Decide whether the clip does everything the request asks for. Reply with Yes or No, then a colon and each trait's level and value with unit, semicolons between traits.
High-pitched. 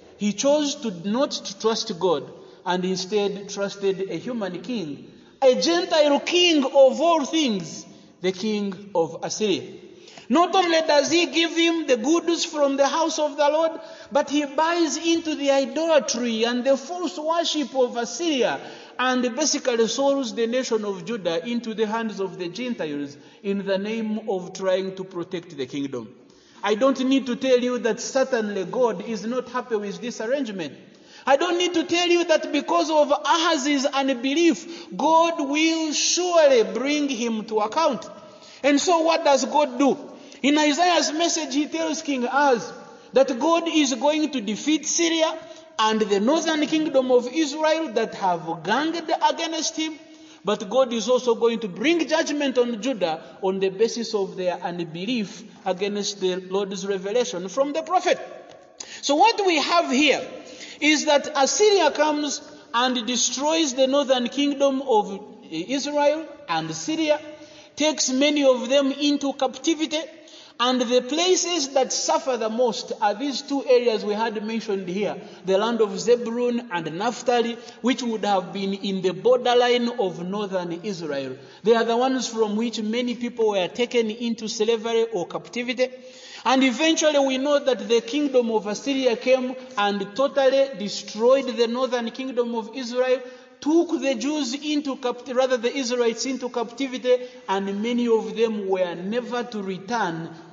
Yes: very high, 255 Hz